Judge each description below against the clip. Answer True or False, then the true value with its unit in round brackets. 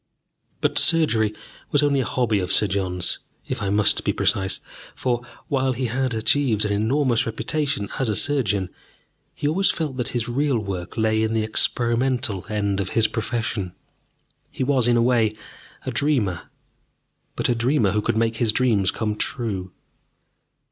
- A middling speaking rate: True (165 wpm)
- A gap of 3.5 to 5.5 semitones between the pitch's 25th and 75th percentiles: True (3.8 semitones)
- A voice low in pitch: True (115 Hz)